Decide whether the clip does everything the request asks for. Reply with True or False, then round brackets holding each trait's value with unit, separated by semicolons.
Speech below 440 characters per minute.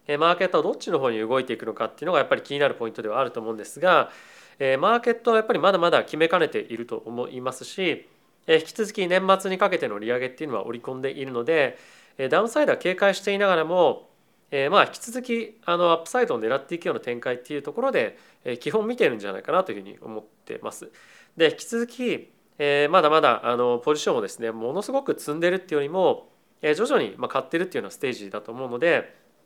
False (470 characters per minute)